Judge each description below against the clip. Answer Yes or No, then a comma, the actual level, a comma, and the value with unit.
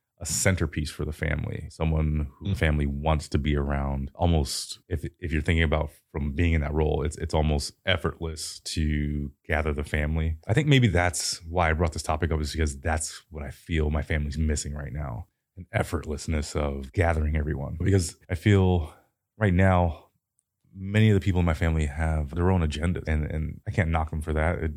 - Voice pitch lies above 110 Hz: No, very low, 80 Hz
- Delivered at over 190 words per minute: Yes, average, 200 wpm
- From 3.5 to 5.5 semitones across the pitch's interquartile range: No, average, 2.7 semitones